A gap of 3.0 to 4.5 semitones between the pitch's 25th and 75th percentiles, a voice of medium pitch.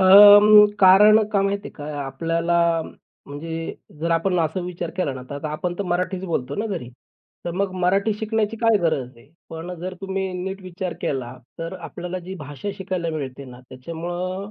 Yes: average, 3.4 semitones; medium, 180 Hz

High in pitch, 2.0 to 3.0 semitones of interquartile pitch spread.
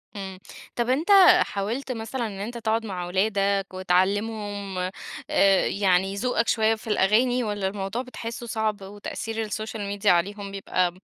Yes: high, 205 Hz; narrow, 2.5 semitones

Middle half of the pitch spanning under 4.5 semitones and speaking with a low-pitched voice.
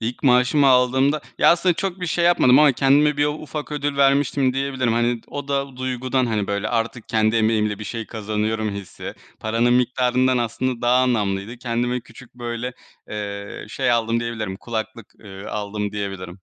Yes: average, 3.4 semitones; low, 120 Hz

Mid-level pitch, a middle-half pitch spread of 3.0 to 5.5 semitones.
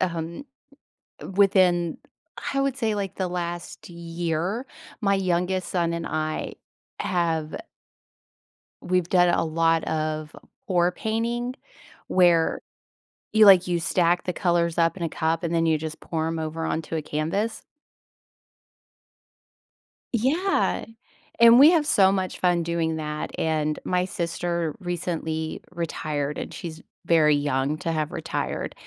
No: medium, 170 Hz; narrow, 2.6 semitones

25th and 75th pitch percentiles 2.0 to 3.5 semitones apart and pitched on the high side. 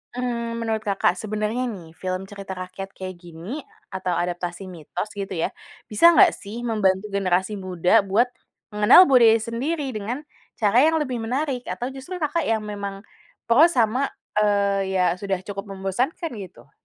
No: average, 4.2 semitones; high, 210 Hz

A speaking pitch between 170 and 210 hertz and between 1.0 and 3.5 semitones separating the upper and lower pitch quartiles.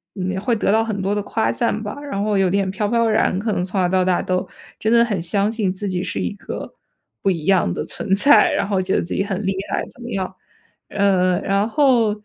Yes: high, 195 Hz; narrow, 2.5 semitones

